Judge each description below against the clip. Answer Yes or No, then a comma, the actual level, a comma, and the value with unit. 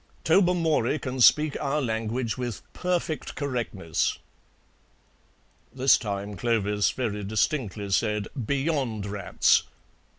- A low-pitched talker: Yes, low, 120 Hz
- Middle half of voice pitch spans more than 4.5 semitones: Yes, wide, 5.5 semitones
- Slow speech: Yes, slow, 95 wpm